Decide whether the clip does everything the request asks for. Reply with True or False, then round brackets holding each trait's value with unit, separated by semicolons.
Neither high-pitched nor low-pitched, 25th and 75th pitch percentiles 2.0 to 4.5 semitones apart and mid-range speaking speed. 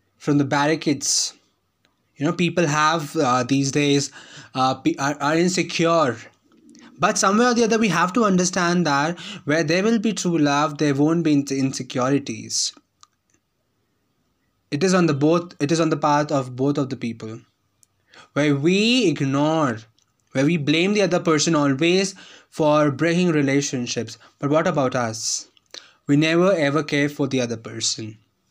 True (150 Hz; 3.9 semitones; 160 wpm)